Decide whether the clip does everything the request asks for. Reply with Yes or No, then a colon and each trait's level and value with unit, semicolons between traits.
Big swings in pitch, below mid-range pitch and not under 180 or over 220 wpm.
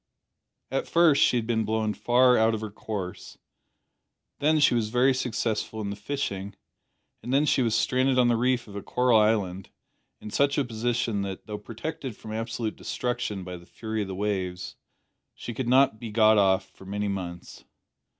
No: average, 3.4 semitones; low, 110 Hz; average, 185 wpm